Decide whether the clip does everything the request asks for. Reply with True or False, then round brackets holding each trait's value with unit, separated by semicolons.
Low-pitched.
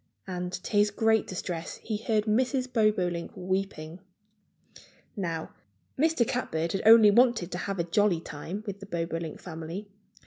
False (195 Hz)